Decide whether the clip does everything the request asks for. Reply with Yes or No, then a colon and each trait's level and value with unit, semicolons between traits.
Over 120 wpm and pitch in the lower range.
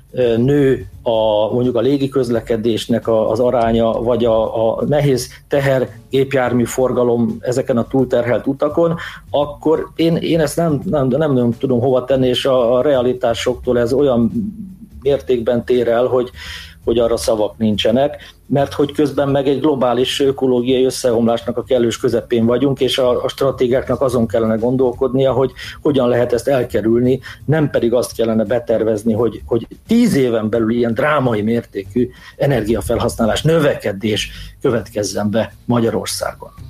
Yes: average, 135 wpm; low, 125 Hz